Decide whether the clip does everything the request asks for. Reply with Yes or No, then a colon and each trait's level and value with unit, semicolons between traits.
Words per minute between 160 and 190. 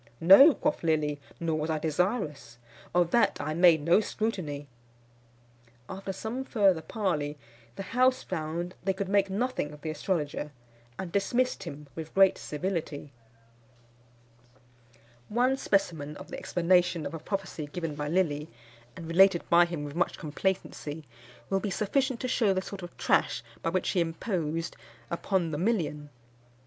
No: average, 150 wpm